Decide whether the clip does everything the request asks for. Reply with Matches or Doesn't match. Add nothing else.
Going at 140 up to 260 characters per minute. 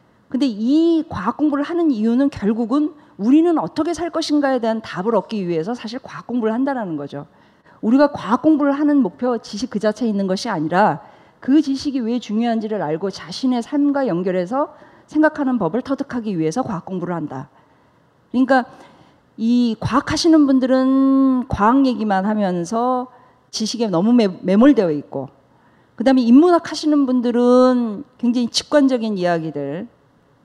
Doesn't match